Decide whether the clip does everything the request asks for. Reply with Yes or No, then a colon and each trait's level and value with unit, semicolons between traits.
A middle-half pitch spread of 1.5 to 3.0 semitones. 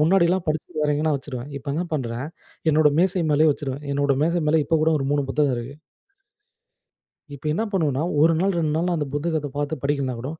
Yes: narrow, 2.5 semitones